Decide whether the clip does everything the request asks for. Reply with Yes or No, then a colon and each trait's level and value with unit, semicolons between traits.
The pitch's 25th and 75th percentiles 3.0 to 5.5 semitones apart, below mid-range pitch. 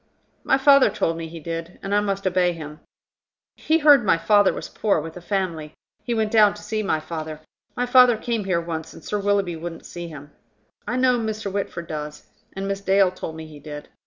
No: average, 4.6 semitones; high, 190 Hz